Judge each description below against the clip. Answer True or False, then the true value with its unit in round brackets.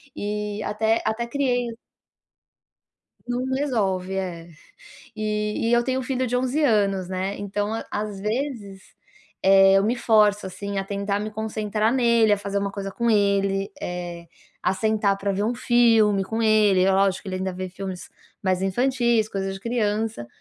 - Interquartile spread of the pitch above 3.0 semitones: False (2.7 semitones)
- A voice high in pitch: True (210 Hz)